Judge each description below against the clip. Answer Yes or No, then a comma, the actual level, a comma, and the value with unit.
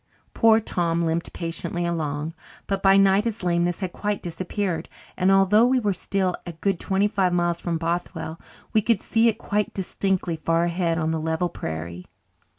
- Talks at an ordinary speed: Yes, average, 175 wpm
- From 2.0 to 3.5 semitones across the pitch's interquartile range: Yes, average, 3.0 semitones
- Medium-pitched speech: Yes, medium, 175 Hz